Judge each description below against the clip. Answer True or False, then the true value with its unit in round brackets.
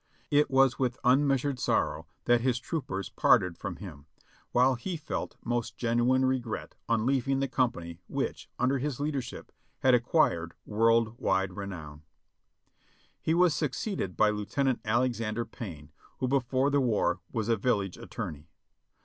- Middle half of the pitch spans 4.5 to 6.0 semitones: True (4.8 semitones)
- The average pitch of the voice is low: True (120 Hz)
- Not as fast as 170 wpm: True (140 wpm)